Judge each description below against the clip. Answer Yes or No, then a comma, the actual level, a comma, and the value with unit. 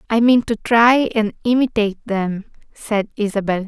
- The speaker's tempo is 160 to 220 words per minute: No, average, 145 wpm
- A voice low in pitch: No, high, 220 Hz